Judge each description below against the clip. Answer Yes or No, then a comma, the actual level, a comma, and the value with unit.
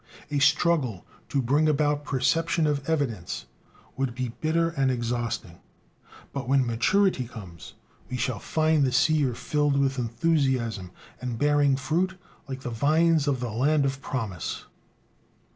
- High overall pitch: No, low, 135 Hz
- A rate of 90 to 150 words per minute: Yes, average, 140 wpm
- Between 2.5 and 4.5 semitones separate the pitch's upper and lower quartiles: Yes, average, 3.8 semitones